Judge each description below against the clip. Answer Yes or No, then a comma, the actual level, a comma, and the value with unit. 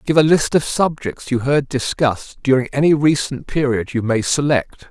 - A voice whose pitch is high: No, low, 135 Hz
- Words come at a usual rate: Yes, average, 185 wpm